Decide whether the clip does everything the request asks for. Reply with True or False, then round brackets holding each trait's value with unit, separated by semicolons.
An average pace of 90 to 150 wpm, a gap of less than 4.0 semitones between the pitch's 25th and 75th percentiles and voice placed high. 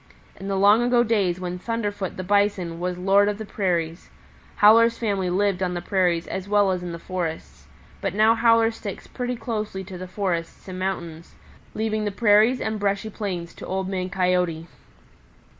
False (180 wpm; 2.9 semitones; 195 Hz)